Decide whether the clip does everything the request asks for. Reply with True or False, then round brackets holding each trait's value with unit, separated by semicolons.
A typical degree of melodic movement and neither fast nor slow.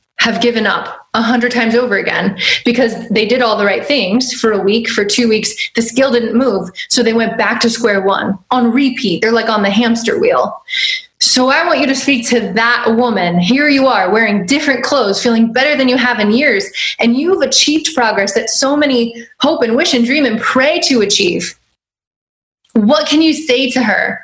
False (3.1 semitones; 210 wpm)